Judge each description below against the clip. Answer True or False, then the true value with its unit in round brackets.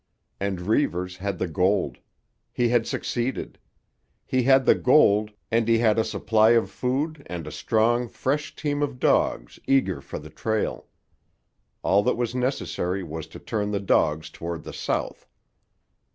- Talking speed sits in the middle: True (155 wpm)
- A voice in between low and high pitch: False (110 Hz)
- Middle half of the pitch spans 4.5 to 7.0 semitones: True (5.2 semitones)